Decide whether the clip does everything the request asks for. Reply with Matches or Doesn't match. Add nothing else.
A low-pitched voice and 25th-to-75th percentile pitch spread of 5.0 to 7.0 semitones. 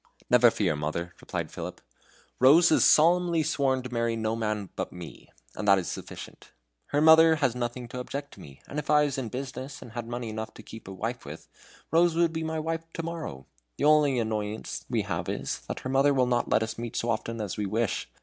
Matches